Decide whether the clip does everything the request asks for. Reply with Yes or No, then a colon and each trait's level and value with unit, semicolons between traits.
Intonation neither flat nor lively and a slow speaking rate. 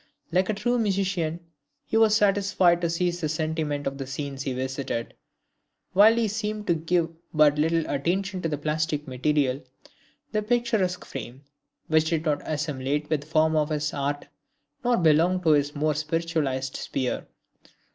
No: average, 4.0 semitones; average, 160 wpm